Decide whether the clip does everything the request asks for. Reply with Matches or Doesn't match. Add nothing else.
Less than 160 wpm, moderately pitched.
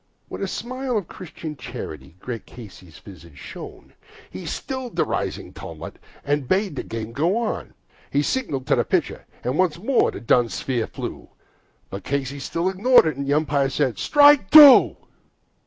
Doesn't match